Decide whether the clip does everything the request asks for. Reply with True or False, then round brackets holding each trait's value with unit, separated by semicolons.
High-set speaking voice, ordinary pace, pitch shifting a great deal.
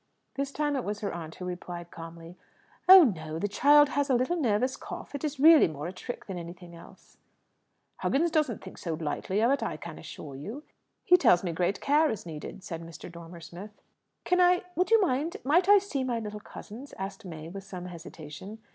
False (205 Hz; 210 wpm; 8.8 semitones)